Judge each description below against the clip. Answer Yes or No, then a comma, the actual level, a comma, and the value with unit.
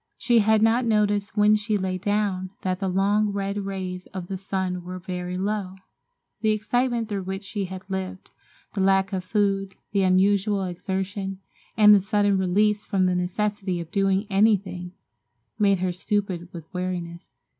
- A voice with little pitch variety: Yes, narrow, 2.1 semitones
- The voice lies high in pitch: Yes, high, 195 Hz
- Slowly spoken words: No, average, 165 wpm